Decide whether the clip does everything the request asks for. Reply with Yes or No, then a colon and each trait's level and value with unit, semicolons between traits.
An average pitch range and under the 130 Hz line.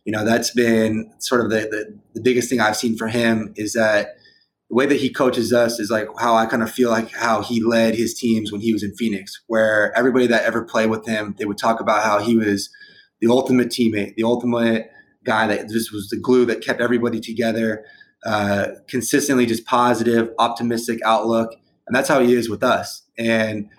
No: narrow, 1.5 semitones; low, 115 Hz